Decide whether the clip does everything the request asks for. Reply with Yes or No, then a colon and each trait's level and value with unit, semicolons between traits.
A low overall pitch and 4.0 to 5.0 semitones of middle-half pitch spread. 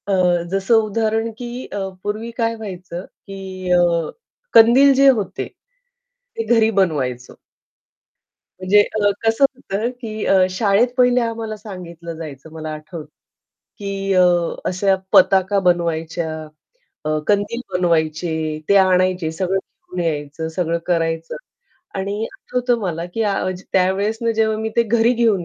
No: high, 195 Hz; average, 4.7 semitones